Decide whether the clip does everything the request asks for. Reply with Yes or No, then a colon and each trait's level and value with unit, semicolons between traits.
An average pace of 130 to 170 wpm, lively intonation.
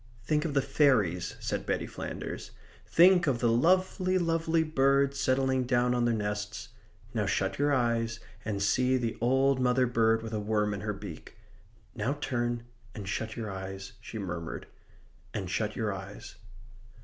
No: average, 160 wpm; average, 4.7 semitones